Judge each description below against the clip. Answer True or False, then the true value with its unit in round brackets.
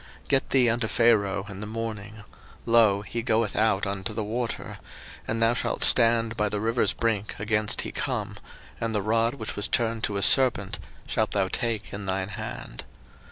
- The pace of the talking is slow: False (185 wpm)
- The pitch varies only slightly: True (2.1 semitones)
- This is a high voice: False (110 Hz)